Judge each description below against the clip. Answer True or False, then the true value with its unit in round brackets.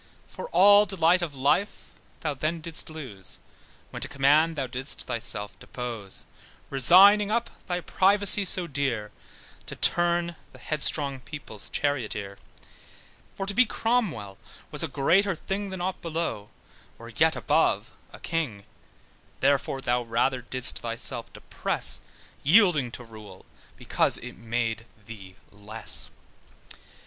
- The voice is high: False (140 Hz)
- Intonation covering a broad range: True (7.4 semitones)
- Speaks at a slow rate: True (130 wpm)